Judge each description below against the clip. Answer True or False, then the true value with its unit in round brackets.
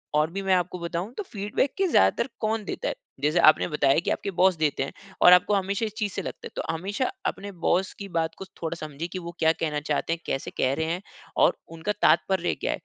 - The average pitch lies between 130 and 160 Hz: False (180 Hz)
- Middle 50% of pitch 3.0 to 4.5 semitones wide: True (3.8 semitones)